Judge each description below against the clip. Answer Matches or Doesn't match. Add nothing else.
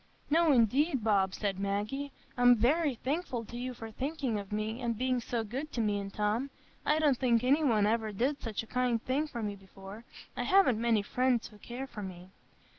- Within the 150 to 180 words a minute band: Doesn't match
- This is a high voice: Matches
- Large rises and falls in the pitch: Doesn't match